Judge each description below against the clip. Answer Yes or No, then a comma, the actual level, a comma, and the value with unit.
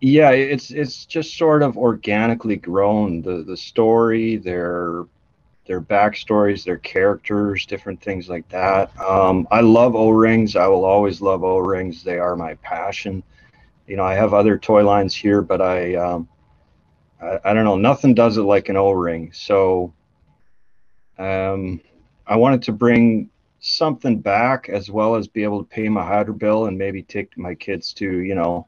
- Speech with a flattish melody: No, average, 3.3 semitones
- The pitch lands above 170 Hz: No, low, 100 Hz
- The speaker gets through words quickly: No, average, 175 wpm